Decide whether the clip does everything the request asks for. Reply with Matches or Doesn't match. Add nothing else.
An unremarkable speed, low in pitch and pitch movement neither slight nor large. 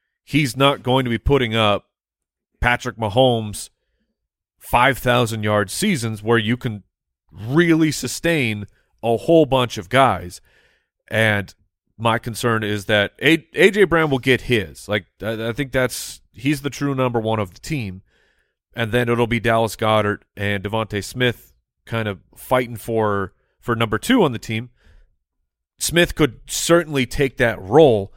Matches